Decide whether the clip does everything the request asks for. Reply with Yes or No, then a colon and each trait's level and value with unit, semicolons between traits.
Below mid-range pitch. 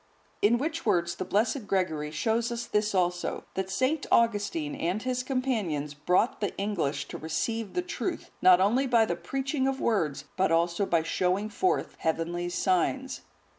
No: high, 200 Hz